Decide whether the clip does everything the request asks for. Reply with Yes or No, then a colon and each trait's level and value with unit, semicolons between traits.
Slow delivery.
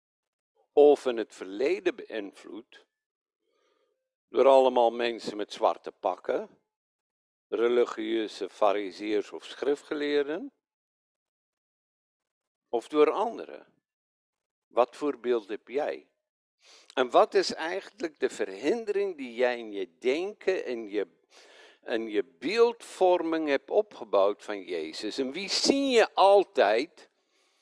Yes: slow, 105 wpm